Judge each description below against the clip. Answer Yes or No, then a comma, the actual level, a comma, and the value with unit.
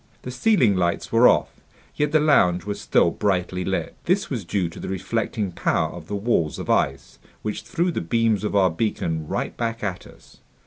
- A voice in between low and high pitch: No, low, 100 Hz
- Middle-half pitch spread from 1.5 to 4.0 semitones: No, average, 4.6 semitones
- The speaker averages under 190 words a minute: No, average, 195 wpm